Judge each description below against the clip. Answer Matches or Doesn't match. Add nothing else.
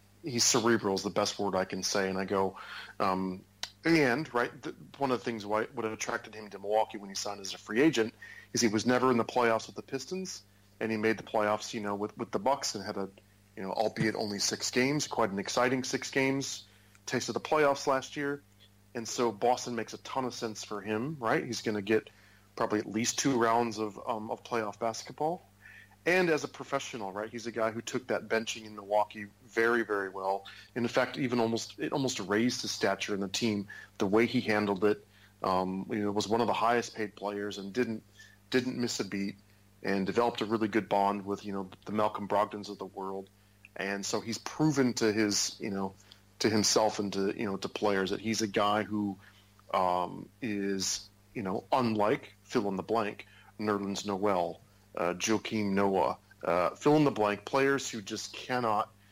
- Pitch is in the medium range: Doesn't match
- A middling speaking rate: Doesn't match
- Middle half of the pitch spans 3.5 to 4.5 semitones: Doesn't match